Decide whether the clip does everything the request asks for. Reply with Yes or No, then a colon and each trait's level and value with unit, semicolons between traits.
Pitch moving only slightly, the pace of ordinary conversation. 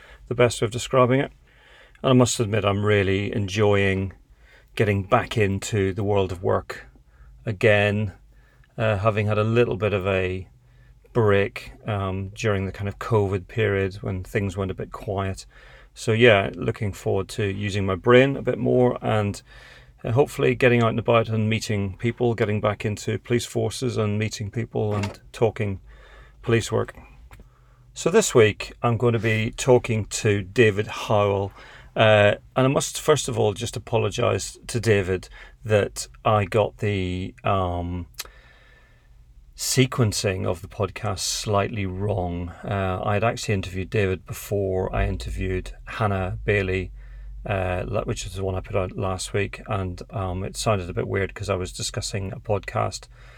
No: average, 3.2 semitones; average, 160 wpm